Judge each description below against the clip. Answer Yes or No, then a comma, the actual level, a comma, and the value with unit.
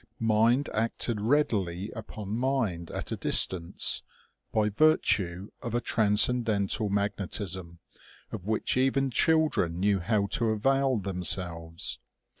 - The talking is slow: Yes, slow, 115 wpm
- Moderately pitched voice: No, low, 105 Hz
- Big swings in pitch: No, average, 4.1 semitones